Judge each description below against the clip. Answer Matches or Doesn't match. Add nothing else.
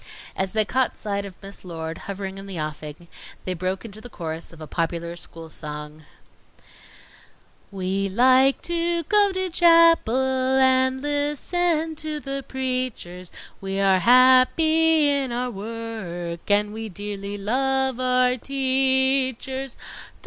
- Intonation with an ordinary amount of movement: Doesn't match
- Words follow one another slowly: Matches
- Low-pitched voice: Doesn't match